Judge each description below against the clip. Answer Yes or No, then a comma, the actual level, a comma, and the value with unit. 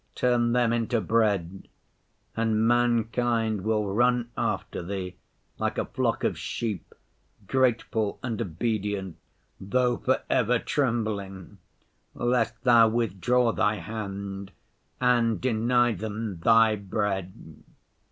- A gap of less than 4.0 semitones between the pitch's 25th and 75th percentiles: Yes, average, 3.1 semitones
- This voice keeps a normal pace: No, slow, 105 wpm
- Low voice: Yes, low, 110 Hz